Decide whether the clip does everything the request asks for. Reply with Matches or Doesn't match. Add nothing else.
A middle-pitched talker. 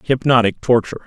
Doesn't match